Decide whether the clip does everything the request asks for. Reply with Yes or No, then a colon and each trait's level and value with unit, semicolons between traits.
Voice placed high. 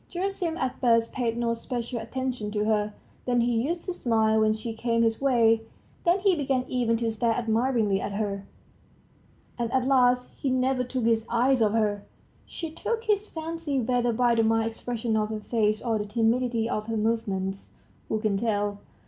Yes: high, 230 Hz